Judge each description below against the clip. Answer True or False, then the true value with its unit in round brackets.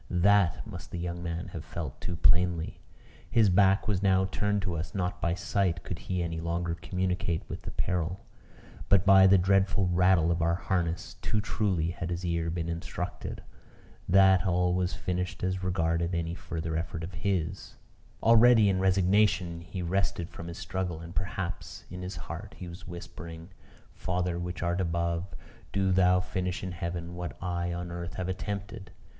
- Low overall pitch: True (90 Hz)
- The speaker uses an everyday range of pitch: False (1.9 semitones)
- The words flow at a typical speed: True (175 wpm)